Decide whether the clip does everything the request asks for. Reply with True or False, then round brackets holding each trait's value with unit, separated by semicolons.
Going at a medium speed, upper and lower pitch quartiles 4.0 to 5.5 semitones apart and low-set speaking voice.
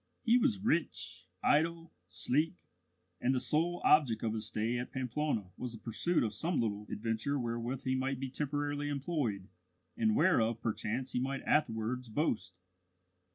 True (155 wpm; 5.2 semitones; 130 Hz)